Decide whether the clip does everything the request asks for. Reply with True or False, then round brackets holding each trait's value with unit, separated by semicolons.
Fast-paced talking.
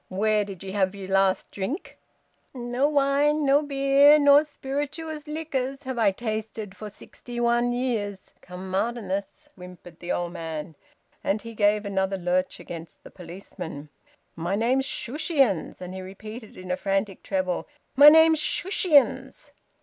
False (145 wpm)